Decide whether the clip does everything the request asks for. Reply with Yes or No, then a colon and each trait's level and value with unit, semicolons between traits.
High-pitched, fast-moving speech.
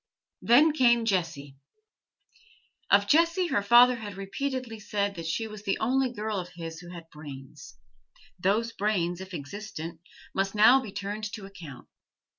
No: high, 200 Hz; average, 150 wpm